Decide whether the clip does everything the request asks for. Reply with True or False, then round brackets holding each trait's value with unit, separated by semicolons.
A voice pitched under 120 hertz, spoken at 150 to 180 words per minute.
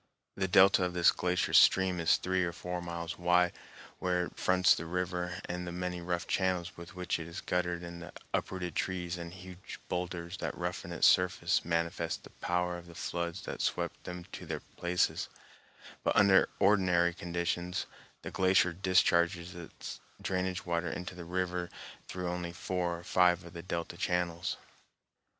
True (90 Hz; 170 wpm)